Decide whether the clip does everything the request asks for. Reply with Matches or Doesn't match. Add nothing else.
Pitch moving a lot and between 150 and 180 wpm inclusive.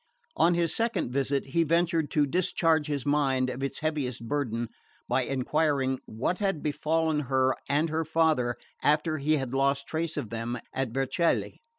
Doesn't match